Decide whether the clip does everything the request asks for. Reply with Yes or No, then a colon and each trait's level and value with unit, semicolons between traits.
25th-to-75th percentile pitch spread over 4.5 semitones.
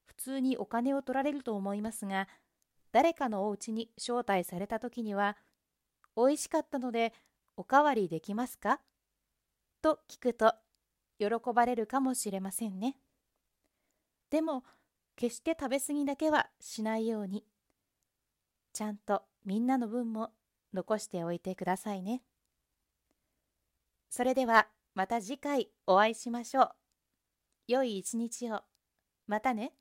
No: average, 4.2 semitones